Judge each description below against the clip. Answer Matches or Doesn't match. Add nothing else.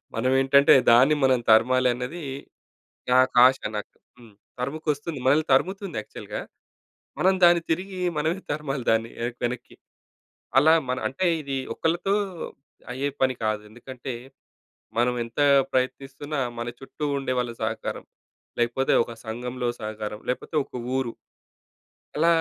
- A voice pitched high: Doesn't match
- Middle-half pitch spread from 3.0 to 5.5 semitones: Matches